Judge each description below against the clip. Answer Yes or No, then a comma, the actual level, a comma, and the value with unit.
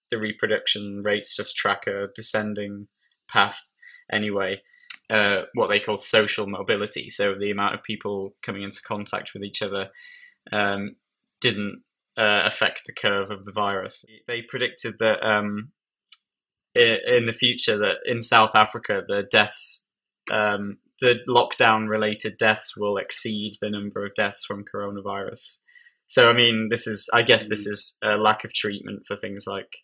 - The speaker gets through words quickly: No, average, 145 wpm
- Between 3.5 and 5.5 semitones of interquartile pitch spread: No, average, 2.7 semitones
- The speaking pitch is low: Yes, low, 105 Hz